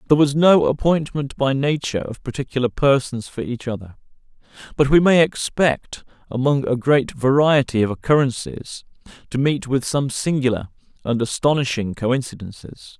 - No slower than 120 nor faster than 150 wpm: Yes, average, 140 wpm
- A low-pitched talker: Yes, low, 130 Hz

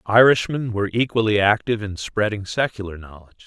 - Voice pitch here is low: Yes, low, 105 Hz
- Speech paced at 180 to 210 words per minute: No, average, 140 wpm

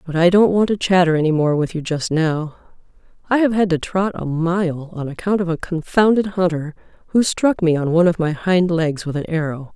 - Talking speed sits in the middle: No, fast, 230 wpm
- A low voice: No, medium, 170 Hz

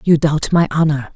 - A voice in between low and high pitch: Yes, medium, 150 Hz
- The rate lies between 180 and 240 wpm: Yes, fast, 205 wpm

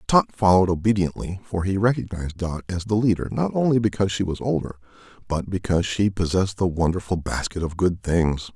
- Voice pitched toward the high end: No, very low, 95 Hz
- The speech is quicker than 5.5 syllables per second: Yes, 6.0 syllables/s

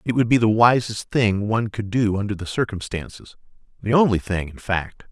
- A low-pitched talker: Yes, low, 105 Hz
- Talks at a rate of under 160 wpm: No, average, 200 wpm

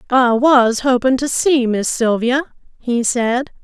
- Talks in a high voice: Yes, very high, 250 Hz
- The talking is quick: No, average, 150 wpm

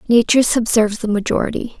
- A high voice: Yes, high, 225 Hz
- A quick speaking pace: No, slow, 135 wpm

